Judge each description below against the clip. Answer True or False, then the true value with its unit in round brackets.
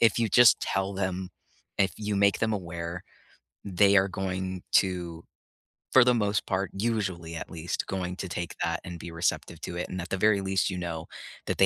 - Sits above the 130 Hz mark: False (95 Hz)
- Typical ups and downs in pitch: False (2.3 semitones)